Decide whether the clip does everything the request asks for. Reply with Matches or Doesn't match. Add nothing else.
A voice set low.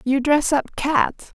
Doesn't match